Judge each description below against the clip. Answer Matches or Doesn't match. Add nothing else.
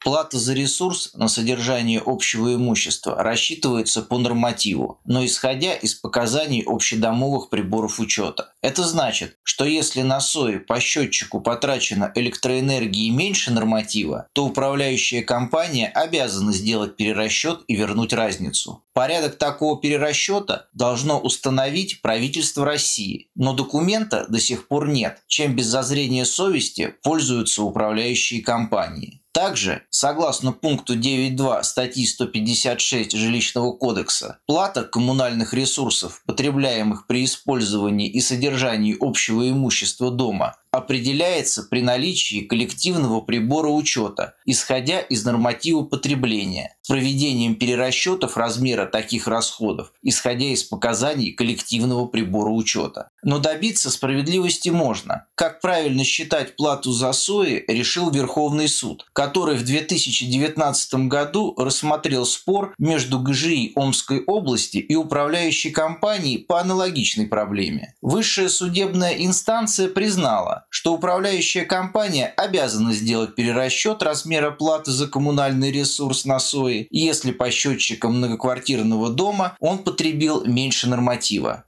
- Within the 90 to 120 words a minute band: Matches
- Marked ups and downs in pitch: Doesn't match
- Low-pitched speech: Matches